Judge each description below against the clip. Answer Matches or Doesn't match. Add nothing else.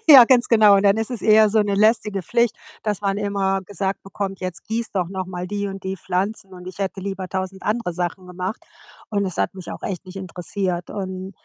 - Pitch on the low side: Doesn't match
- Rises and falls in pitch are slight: Matches